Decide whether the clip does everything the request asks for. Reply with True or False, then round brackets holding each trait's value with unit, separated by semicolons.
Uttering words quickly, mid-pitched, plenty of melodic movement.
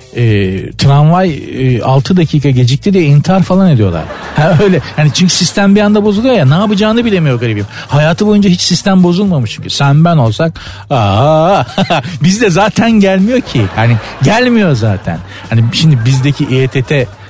True (155 wpm; 150 Hz; 7.2 semitones)